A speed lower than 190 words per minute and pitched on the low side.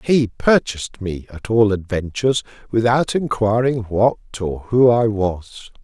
Yes: slow, 135 wpm; low, 110 Hz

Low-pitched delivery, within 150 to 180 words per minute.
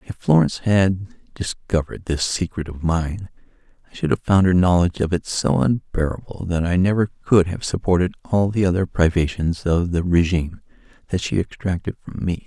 Yes: very low, 90 Hz; average, 175 wpm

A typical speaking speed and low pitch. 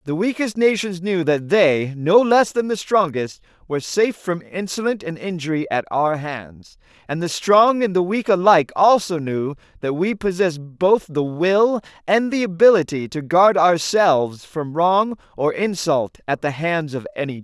No: average, 175 wpm; medium, 175 Hz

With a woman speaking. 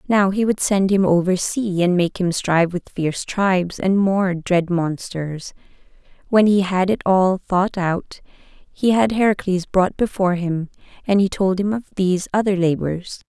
Yes: female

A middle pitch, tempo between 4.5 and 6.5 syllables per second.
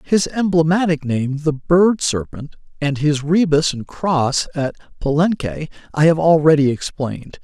No: medium, 155 Hz; 4.2 syllables/s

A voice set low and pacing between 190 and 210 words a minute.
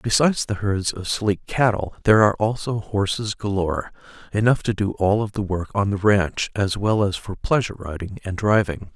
Yes: low, 100 Hz; average, 195 wpm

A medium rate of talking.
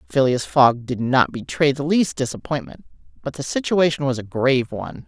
Yes: average, 175 wpm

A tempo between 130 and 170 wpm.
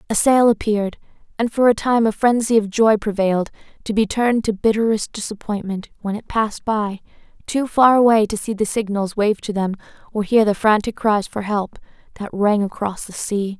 No: average, 195 wpm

